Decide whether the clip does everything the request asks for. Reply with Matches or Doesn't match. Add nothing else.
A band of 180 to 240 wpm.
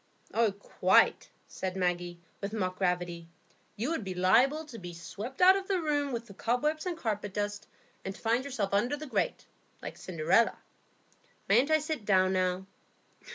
Doesn't match